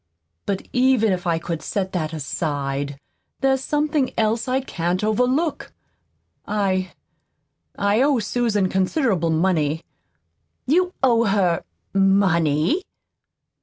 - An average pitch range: No, wide, 6.7 semitones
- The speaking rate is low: Yes, slow, 105 wpm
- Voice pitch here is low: No, high, 200 Hz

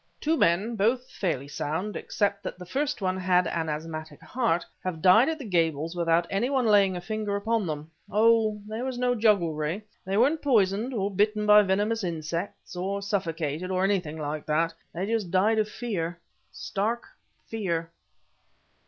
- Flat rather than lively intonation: No, average, 4.5 semitones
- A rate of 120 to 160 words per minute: No, average, 170 wpm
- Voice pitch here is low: No, high, 195 Hz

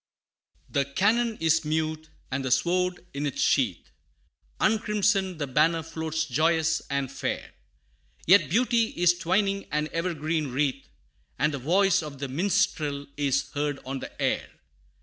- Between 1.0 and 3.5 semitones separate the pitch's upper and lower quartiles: No, average, 4.3 semitones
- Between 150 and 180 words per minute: No, average, 140 wpm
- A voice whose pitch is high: No, medium, 160 Hz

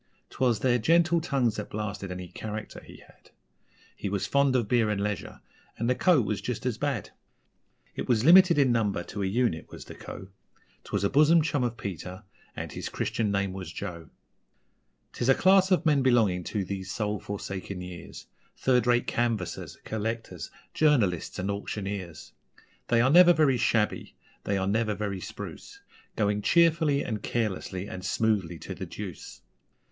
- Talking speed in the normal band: Yes, average, 170 wpm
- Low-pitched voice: Yes, low, 110 Hz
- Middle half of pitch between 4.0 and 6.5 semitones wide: Yes, average, 4.8 semitones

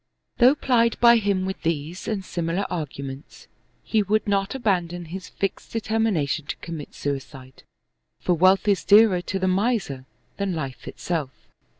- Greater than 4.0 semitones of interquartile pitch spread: Yes, average, 4.6 semitones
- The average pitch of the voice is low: No, medium, 185 Hz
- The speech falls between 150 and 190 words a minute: Yes, average, 155 wpm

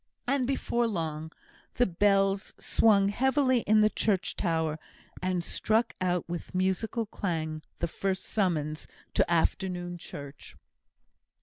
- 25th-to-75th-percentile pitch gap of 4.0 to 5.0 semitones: Yes, average, 4.3 semitones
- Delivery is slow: Yes, slow, 120 wpm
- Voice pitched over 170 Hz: Yes, medium, 185 Hz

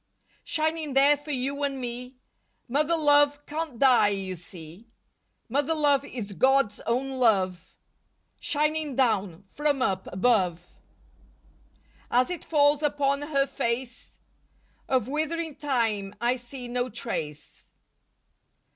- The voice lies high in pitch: Yes, very high, 260 Hz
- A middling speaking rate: No, slow, 115 wpm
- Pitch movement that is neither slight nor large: Yes, average, 4.6 semitones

